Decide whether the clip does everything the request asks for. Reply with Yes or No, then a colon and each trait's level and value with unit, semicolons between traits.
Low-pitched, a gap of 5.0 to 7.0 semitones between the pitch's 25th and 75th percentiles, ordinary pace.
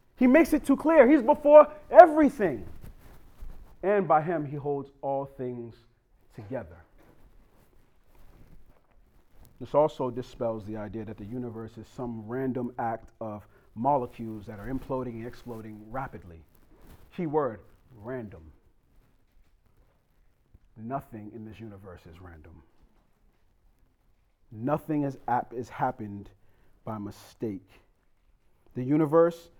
No: low, 115 Hz; average, 5.3 semitones; slow, 105 wpm